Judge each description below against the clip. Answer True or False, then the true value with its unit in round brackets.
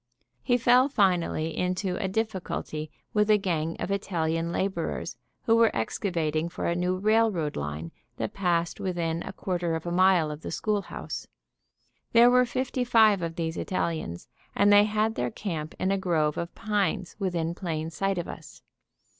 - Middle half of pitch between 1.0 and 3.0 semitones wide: False (4.1 semitones)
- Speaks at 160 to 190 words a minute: True (165 wpm)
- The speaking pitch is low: False (180 Hz)